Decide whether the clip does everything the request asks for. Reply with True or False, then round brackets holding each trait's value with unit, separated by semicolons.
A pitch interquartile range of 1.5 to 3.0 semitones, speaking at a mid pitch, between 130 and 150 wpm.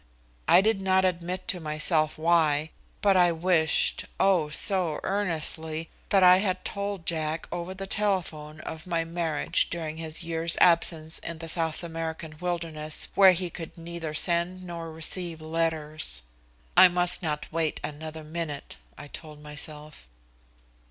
True (2.4 semitones; 165 Hz; 145 wpm)